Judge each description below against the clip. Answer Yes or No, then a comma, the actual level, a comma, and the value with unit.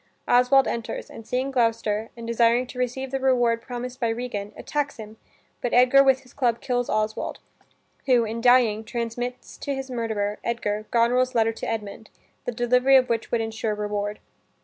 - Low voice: No, high, 235 Hz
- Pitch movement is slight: Yes, narrow, 2.1 semitones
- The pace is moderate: Yes, average, 170 wpm